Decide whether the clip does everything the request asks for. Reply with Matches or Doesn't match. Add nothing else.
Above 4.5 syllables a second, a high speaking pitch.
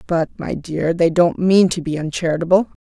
Doesn't match